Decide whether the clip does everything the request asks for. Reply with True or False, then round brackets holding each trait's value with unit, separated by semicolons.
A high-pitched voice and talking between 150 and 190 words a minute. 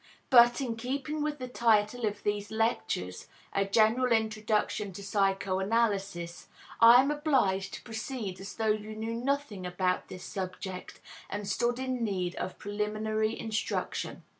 False (215 Hz; 140 wpm)